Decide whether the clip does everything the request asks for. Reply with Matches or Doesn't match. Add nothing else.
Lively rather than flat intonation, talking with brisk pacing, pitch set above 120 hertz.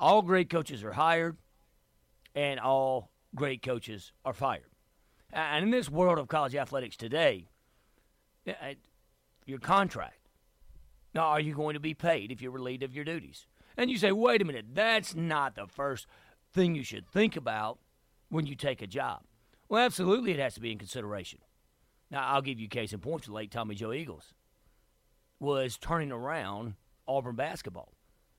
Doesn't match